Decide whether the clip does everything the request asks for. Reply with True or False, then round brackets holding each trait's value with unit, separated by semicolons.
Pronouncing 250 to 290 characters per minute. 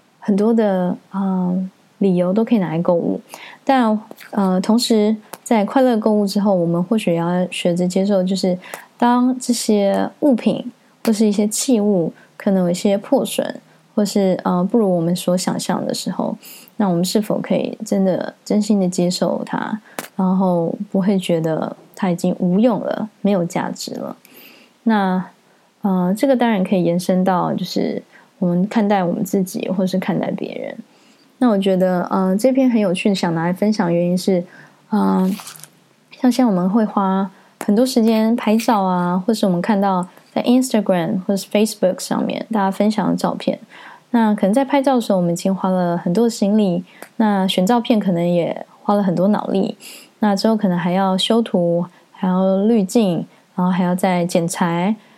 True (270 characters per minute)